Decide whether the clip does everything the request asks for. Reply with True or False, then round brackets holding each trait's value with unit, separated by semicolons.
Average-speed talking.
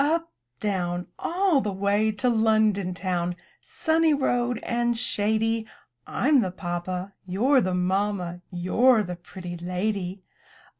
False (130 wpm)